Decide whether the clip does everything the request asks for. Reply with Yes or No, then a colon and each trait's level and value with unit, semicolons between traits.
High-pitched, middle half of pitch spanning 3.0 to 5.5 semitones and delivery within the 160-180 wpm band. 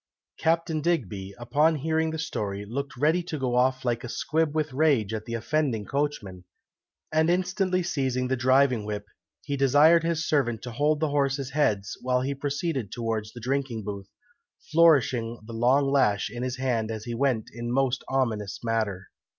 No: low, 130 Hz; average, 4.8 semitones; average, 175 wpm